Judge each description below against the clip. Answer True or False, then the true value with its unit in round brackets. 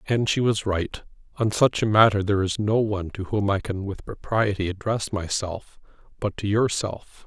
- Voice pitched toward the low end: True (105 Hz)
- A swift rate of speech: False (190 wpm)